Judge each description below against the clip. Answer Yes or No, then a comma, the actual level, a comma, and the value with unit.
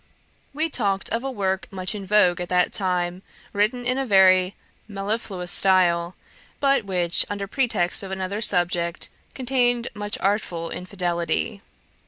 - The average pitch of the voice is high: Yes, high, 195 Hz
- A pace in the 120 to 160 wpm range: Yes, average, 140 wpm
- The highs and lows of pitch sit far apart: No, average, 3.3 semitones